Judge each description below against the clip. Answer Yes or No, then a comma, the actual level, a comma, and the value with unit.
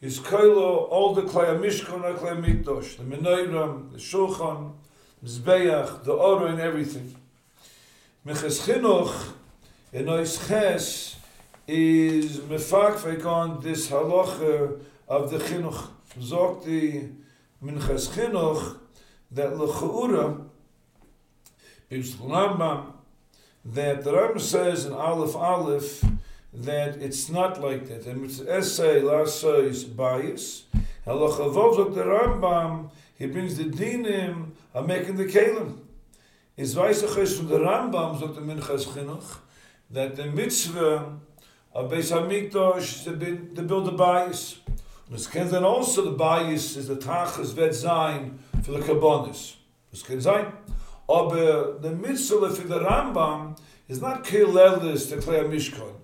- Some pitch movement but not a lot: Yes, average, 4.2 semitones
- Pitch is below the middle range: No, medium, 155 Hz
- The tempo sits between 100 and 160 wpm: Yes, slow, 135 wpm